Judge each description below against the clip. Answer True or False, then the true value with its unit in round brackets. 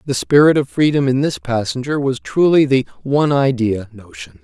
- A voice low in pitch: True (130 Hz)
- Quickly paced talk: False (175 wpm)